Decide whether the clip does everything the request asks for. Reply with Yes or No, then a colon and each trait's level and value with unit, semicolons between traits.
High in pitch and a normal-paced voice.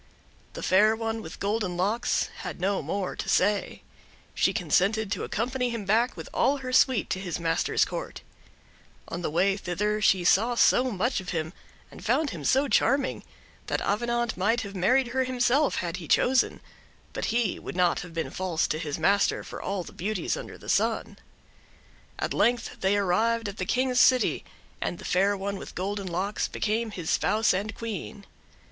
Yes: high, 205 Hz; average, 180 wpm